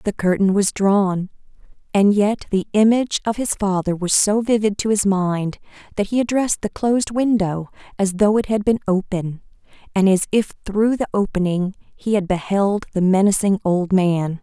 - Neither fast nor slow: Yes, average, 175 wpm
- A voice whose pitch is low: No, high, 200 Hz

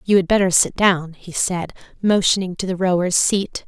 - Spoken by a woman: Yes, female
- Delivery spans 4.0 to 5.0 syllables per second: Yes, 4.9 syllables/s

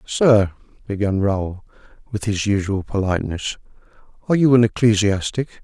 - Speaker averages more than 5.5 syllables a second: No, 5.1 syllables/s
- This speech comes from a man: Yes, male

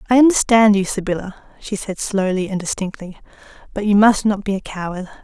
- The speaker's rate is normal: Yes, average, 185 wpm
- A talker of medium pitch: No, high, 200 Hz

